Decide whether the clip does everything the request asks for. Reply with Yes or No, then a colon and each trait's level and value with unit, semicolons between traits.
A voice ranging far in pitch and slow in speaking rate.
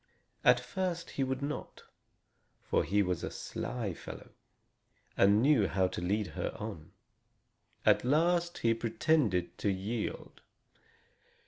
Yes: wide, 6.8 semitones; slow, 125 wpm